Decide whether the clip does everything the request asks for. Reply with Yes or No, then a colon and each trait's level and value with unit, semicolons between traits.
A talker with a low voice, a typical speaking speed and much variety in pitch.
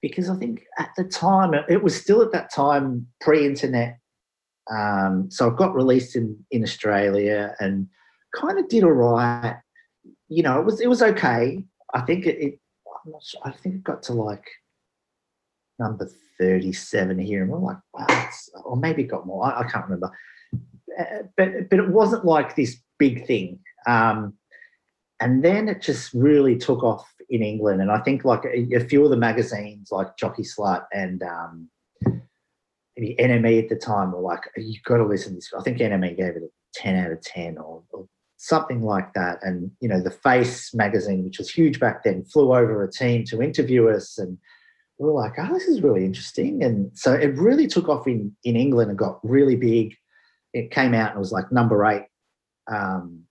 Yes: low, 120 Hz; average, 195 wpm; wide, 6.8 semitones